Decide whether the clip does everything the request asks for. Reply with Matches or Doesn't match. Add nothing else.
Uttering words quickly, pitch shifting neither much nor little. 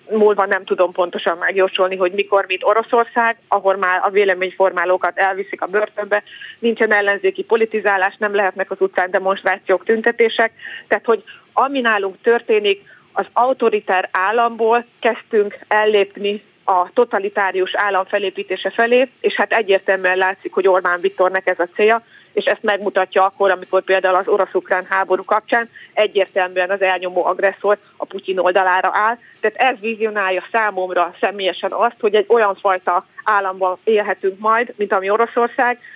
Doesn't match